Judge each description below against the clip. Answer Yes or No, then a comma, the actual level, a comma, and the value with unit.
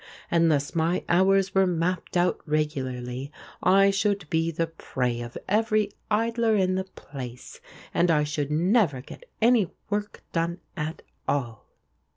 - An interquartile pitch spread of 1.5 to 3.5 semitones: No, average, 4.8 semitones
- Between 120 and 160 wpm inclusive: Yes, average, 140 wpm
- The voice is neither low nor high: Yes, medium, 170 Hz